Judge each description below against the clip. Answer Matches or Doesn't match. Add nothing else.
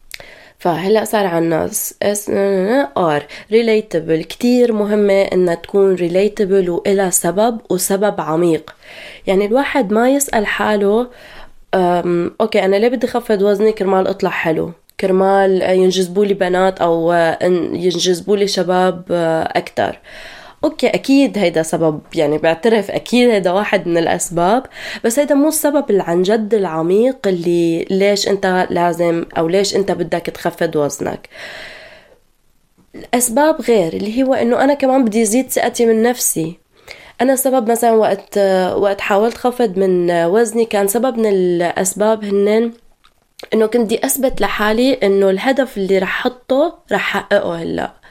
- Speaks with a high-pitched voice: Matches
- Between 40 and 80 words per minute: Doesn't match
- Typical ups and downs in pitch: Matches